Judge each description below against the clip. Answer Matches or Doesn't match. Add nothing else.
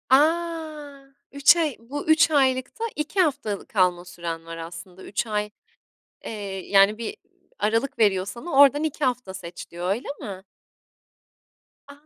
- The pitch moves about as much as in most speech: Doesn't match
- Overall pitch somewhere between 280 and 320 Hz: Doesn't match